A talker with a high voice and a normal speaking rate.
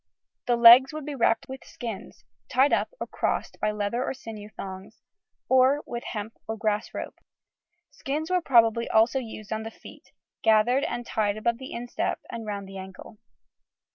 Yes: high, 230 Hz; average, 170 wpm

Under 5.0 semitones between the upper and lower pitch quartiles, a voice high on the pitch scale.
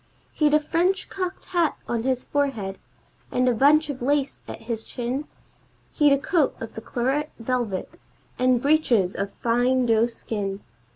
Yes: average, 4.3 semitones; very high, 255 Hz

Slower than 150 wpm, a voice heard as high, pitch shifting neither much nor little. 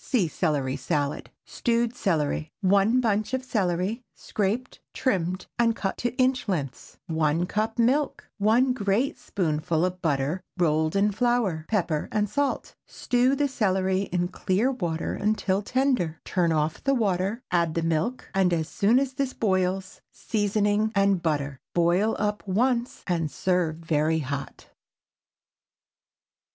No: average, 140 wpm; high, 195 Hz; wide, 5.8 semitones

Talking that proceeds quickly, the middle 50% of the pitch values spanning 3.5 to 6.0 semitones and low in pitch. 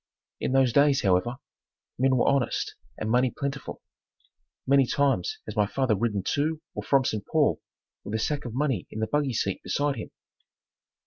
No: average, 175 wpm; average, 4.2 semitones; low, 130 Hz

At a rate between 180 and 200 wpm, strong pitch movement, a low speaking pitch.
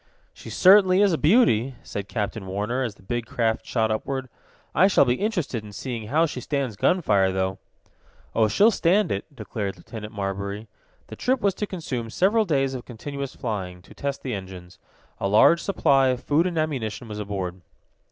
Yes: average, 185 wpm; wide, 7.3 semitones; low, 120 Hz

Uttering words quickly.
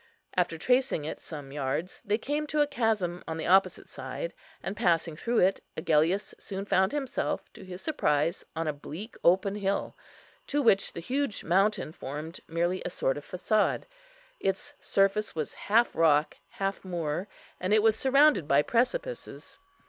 No: average, 165 wpm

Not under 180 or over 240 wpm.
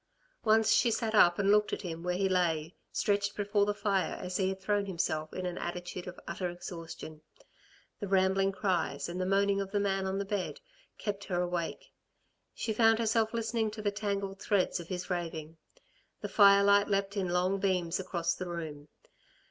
Yes: average, 190 wpm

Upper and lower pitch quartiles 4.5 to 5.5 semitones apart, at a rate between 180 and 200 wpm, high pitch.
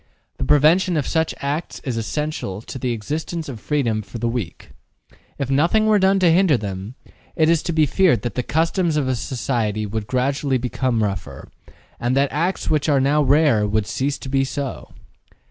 No: average, 5.1 semitones; average, 190 wpm; low, 135 Hz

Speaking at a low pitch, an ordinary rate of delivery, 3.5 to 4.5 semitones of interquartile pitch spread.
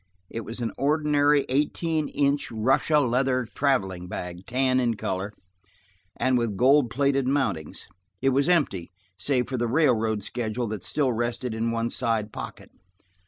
Yes: low, 125 Hz; average, 150 wpm; average, 3.8 semitones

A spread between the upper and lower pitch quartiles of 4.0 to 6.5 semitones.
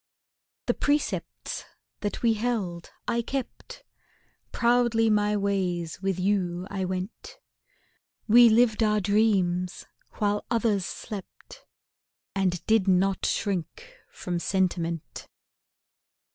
No: average, 3.6 semitones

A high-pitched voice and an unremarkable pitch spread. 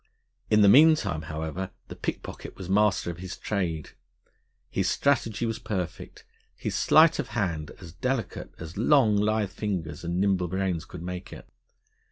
No: very low, 95 Hz; average, 4.1 semitones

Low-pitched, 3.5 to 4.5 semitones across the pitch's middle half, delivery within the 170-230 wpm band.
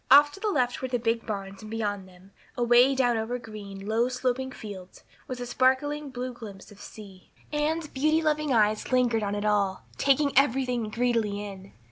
No: high, 240 Hz; average, 4.1 semitones; average, 185 wpm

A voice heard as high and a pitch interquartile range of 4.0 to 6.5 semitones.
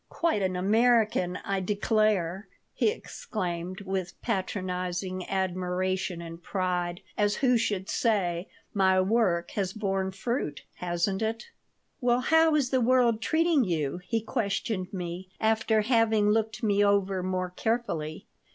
No: high, 195 Hz; average, 3.5 semitones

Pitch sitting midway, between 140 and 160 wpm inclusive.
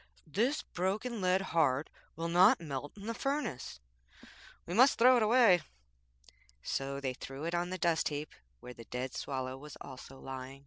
No: medium, 165 Hz; average, 170 wpm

